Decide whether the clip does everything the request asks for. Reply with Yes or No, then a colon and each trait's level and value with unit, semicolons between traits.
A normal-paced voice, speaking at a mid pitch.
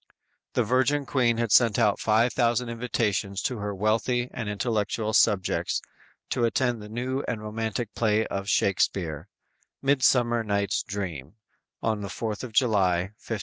No: average, 150 wpm; low, 110 Hz